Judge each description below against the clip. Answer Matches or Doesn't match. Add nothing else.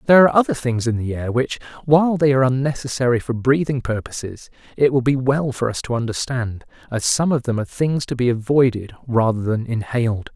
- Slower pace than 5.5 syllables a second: Doesn't match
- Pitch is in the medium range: Doesn't match